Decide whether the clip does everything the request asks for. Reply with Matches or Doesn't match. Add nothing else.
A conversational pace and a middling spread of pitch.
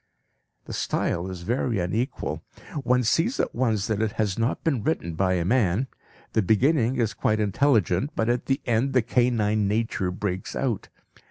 Matches